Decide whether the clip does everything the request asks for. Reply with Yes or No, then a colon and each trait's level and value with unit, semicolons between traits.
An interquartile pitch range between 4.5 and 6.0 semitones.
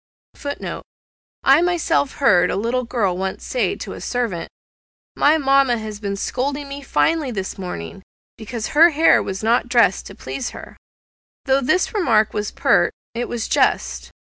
Yes: wide, 5.5 semitones